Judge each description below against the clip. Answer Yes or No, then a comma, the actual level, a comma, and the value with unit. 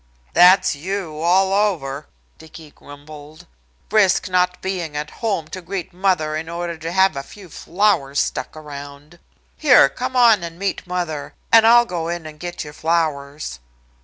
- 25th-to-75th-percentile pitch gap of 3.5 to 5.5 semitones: Yes, average, 3.9 semitones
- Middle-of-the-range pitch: Yes, medium, 170 Hz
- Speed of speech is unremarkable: Yes, average, 160 wpm